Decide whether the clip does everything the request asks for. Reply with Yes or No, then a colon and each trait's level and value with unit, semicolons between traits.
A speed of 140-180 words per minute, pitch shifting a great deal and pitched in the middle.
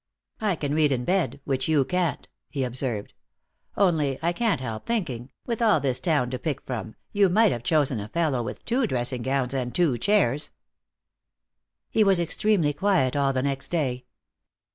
Yes: average, 175 wpm; wide, 5.9 semitones; medium, 145 Hz